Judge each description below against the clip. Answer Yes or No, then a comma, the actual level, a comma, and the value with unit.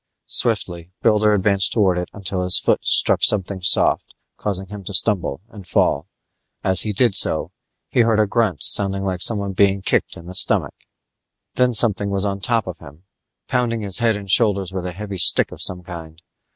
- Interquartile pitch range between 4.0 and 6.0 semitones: No, narrow, 2.5 semitones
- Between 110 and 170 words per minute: No, average, 190 wpm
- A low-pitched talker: Yes, low, 100 Hz